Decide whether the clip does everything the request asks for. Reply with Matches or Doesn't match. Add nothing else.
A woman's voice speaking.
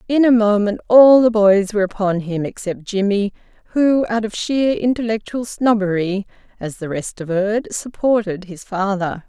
Matches